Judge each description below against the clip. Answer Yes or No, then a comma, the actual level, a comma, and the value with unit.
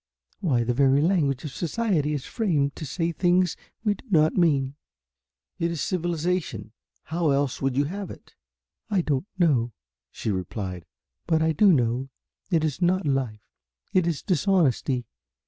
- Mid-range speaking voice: Yes, medium, 155 Hz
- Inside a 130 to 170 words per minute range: Yes, average, 155 wpm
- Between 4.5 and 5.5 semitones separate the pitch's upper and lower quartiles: Yes, average, 4.8 semitones